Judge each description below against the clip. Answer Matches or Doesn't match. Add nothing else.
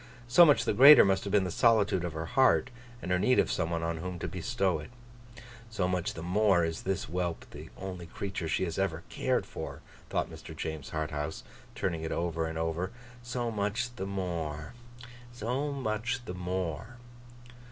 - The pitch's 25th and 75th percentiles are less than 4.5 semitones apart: Doesn't match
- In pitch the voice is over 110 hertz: Doesn't match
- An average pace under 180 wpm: Doesn't match